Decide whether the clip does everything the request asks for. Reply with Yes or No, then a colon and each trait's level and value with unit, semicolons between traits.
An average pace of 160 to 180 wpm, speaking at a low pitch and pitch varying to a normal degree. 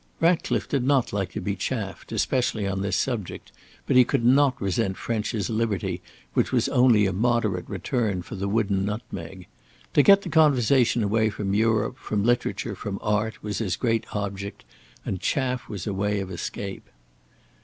Yes: average, 170 wpm; low, 105 Hz; average, 3.7 semitones